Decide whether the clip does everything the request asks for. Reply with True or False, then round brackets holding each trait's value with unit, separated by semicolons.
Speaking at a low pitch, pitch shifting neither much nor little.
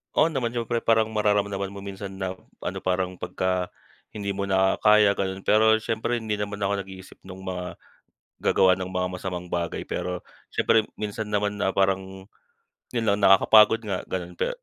False (100 Hz; 2.2 semitones)